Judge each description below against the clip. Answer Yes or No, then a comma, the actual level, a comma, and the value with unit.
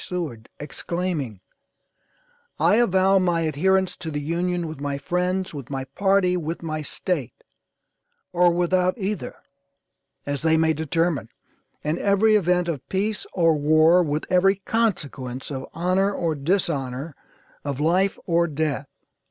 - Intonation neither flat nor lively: Yes, average, 3.9 semitones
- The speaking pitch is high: No, medium, 170 Hz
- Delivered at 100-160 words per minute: Yes, slow, 135 wpm